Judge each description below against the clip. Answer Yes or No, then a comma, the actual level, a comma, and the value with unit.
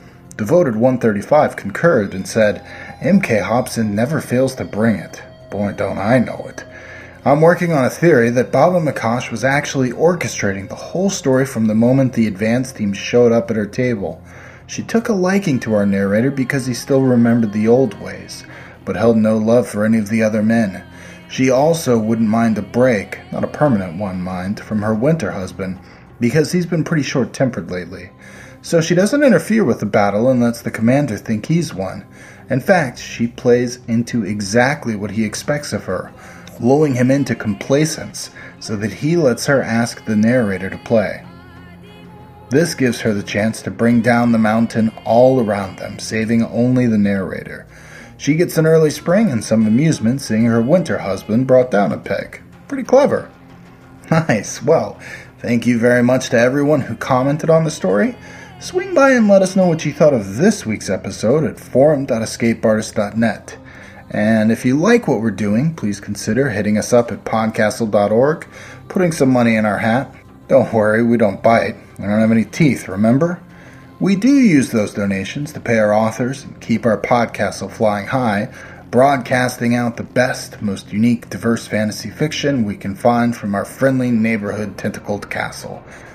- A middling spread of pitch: Yes, average, 4.1 semitones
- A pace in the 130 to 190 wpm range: Yes, average, 175 wpm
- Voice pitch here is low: Yes, low, 115 Hz